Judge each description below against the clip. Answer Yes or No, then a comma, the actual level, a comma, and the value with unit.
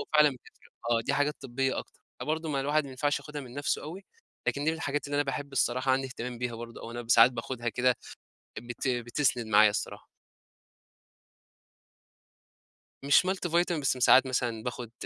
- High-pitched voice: No, low, 130 Hz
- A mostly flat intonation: No, average, 3.3 semitones